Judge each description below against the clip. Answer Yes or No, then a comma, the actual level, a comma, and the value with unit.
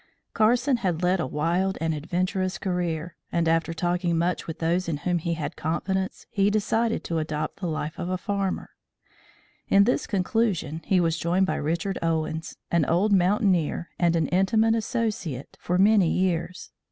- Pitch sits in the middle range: Yes, medium, 180 Hz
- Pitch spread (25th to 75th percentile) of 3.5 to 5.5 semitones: No, average, 3.0 semitones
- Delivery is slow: No, average, 165 wpm